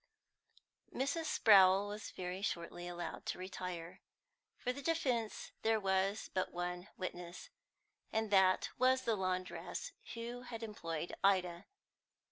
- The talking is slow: Yes, slow, 120 wpm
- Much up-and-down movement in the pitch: No, average, 3.9 semitones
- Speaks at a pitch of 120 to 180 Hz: No, high, 195 Hz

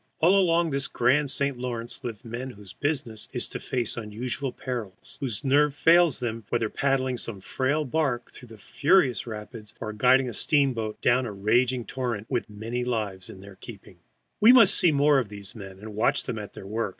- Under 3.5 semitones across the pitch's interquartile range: No, average, 4.3 semitones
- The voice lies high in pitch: No, low, 120 Hz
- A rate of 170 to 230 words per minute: Yes, average, 200 wpm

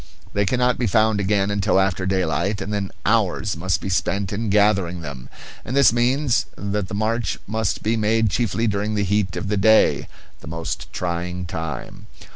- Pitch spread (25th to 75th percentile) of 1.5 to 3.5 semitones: Yes, average, 3.0 semitones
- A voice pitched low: Yes, low, 100 Hz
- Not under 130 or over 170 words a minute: No, average, 180 wpm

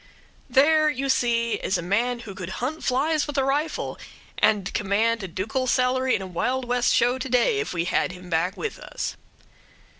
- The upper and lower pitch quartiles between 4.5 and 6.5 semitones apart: Yes, average, 5.2 semitones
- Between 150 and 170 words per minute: No, average, 190 wpm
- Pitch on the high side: Yes, high, 245 Hz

